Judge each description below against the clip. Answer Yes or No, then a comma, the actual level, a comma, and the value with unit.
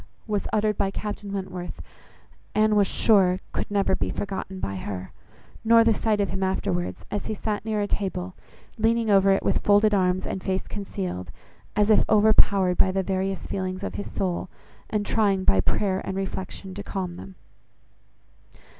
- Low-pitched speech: No, high, 195 Hz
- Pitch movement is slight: Yes, narrow, 1.9 semitones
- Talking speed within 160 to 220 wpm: Yes, average, 170 wpm